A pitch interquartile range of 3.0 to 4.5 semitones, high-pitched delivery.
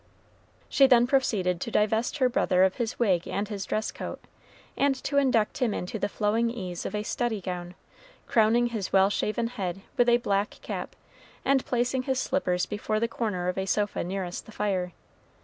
Yes: average, 3.9 semitones; high, 215 Hz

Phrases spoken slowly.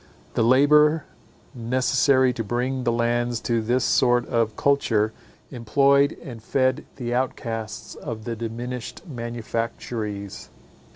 Yes: slow, 115 wpm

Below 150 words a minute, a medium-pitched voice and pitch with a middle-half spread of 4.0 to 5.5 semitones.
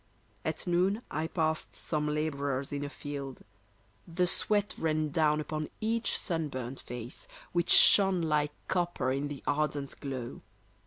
No: average, 140 wpm; medium, 150 Hz; average, 3.5 semitones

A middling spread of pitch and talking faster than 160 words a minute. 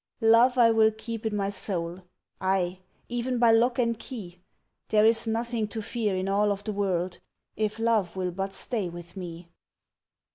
Yes: average, 3.5 semitones; average, 175 wpm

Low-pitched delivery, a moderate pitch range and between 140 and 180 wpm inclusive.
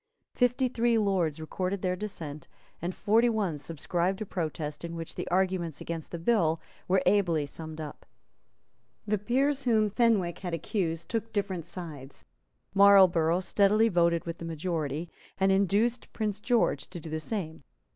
No: medium, 185 Hz; average, 4.3 semitones; average, 155 wpm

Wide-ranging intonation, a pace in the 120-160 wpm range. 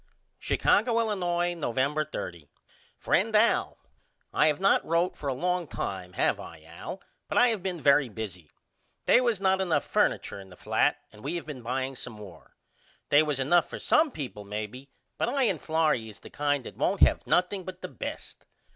No: wide, 8.3 semitones; average, 185 wpm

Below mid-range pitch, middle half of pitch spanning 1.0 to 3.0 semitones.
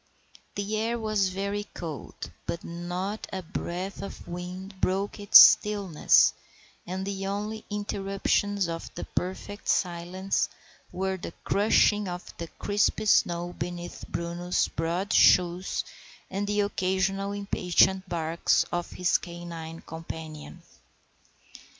No: high, 190 Hz; average, 2.7 semitones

